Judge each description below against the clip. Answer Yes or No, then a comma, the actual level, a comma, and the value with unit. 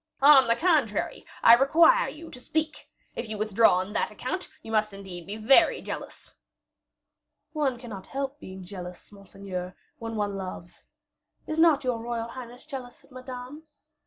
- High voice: Yes, high, 235 Hz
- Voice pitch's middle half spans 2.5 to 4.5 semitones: No, wide, 5.5 semitones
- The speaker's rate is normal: Yes, average, 160 wpm